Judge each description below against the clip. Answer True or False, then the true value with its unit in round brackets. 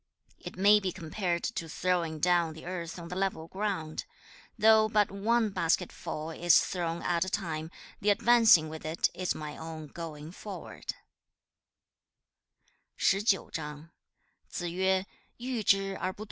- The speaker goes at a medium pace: False (115 wpm)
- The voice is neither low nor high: True (175 Hz)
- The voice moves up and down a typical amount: True (3.6 semitones)